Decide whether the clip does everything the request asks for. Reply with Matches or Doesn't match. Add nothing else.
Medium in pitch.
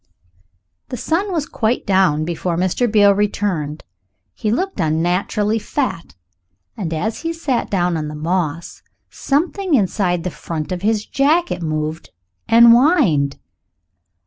Doesn't match